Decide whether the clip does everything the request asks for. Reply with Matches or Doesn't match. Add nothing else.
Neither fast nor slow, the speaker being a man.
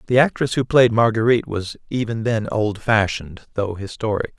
Matches